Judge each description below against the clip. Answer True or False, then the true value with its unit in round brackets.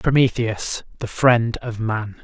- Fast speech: False (135 wpm)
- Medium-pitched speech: False (115 Hz)